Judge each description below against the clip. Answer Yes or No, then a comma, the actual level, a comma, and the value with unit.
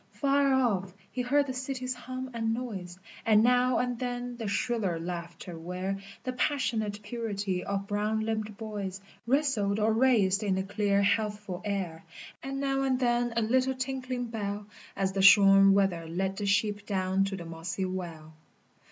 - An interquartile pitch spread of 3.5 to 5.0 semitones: Yes, average, 4.2 semitones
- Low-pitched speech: No, high, 210 Hz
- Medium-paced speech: Yes, average, 165 wpm